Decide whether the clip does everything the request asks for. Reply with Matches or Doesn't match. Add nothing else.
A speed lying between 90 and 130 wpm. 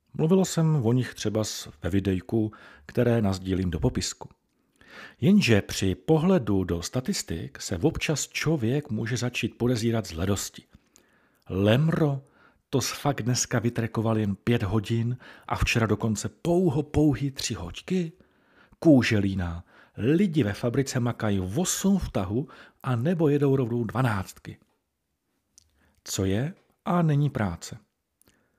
Matches